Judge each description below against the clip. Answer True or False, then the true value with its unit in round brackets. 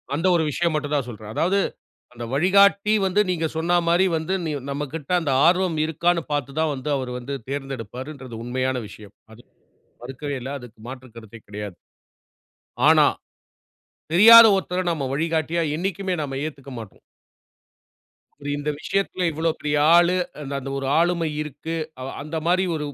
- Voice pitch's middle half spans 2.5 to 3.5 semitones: False (4.7 semitones)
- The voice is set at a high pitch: False (150 Hz)